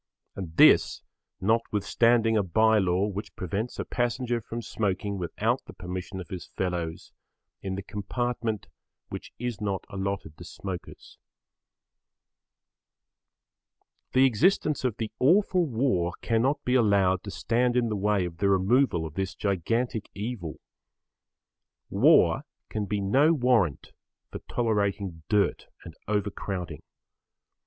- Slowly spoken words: Yes, slow, 125 wpm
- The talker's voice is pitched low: Yes, low, 105 Hz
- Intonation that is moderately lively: Yes, average, 3.9 semitones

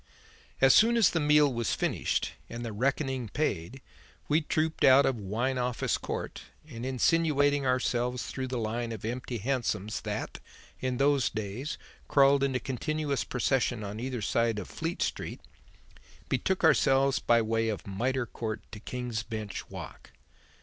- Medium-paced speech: Yes, average, 155 wpm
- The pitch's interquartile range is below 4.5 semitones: Yes, average, 3.4 semitones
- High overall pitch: No, low, 125 Hz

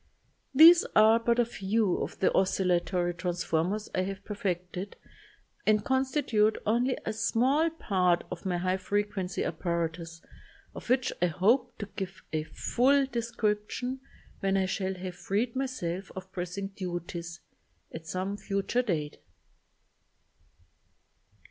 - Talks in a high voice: Yes, high, 195 Hz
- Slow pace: Yes, slow, 130 wpm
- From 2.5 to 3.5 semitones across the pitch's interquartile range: No, average, 4.4 semitones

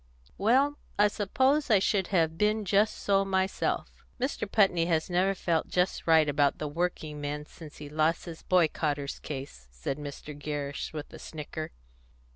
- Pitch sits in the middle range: Yes, medium, 165 Hz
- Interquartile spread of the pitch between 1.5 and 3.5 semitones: No, average, 4.8 semitones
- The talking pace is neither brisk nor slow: Yes, average, 160 wpm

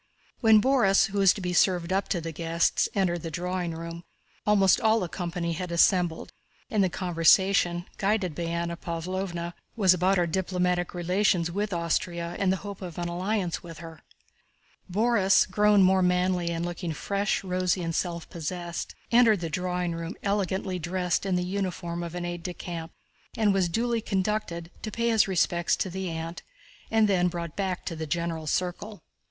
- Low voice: No, medium, 180 Hz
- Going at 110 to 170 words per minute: No, average, 180 wpm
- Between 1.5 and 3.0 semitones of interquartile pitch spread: Yes, narrow, 2.4 semitones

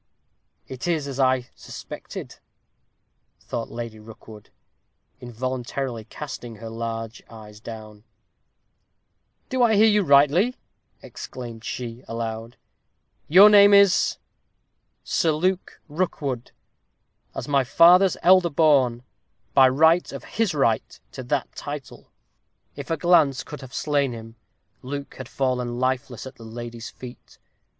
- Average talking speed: No, slow, 125 wpm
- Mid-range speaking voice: No, low, 130 Hz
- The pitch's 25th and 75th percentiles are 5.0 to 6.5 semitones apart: Yes, wide, 5.5 semitones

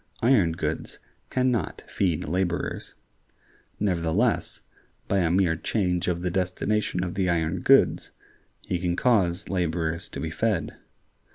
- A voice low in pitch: Yes, very low, 90 Hz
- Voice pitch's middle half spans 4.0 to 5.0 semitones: No, average, 2.8 semitones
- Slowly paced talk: Yes, slow, 130 wpm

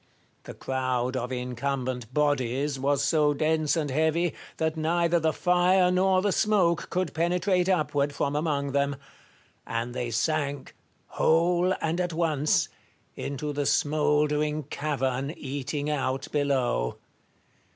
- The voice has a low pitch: No, medium, 150 Hz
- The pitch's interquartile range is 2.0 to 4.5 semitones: Yes, average, 3.5 semitones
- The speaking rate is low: Yes, slow, 125 wpm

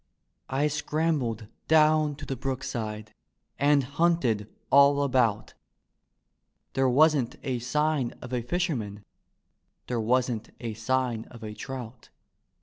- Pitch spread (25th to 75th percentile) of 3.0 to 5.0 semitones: Yes, average, 4.2 semitones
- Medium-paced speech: No, slow, 115 wpm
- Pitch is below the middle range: Yes, low, 130 Hz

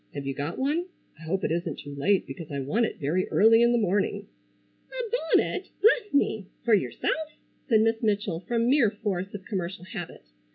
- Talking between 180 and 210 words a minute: Yes, average, 195 wpm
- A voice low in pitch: No, high, 205 Hz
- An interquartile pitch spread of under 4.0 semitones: No, wide, 5.6 semitones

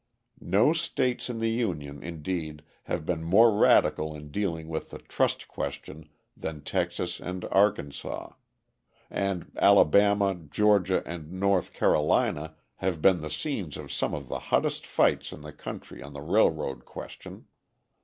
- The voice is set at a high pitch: No, very low, 85 Hz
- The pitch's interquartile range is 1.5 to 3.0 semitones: No, average, 4.7 semitones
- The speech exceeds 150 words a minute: No, average, 145 wpm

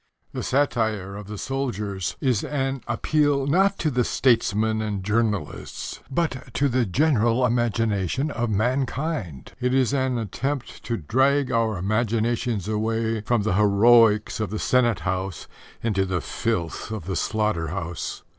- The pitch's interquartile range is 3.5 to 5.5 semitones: Yes, average, 4.0 semitones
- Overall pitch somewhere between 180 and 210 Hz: No, low, 115 Hz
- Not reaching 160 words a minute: Yes, average, 145 wpm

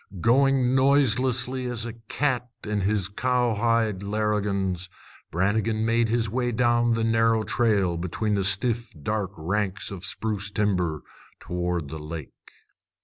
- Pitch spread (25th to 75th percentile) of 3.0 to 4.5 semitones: Yes, average, 3.5 semitones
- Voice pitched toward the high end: No, low, 110 Hz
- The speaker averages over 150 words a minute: No, slow, 135 wpm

